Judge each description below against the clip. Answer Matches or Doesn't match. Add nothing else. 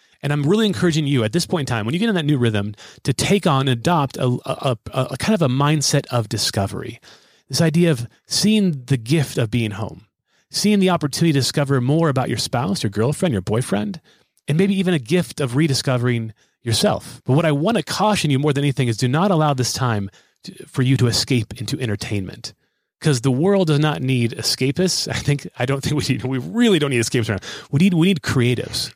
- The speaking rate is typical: Doesn't match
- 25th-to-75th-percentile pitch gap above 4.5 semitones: Matches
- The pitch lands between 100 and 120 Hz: Doesn't match